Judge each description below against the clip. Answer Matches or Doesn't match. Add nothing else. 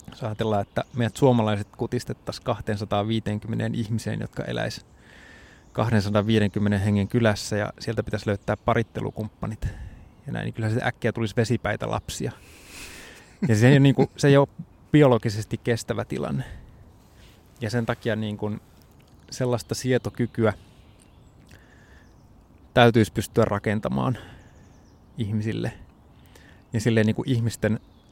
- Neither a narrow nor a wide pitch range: Doesn't match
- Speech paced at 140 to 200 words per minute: Doesn't match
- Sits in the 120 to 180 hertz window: Doesn't match